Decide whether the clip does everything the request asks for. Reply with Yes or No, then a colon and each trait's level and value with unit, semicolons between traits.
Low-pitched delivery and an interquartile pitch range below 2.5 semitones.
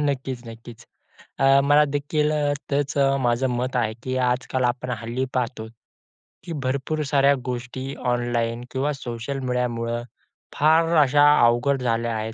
No: low, 130 Hz; average, 2.8 semitones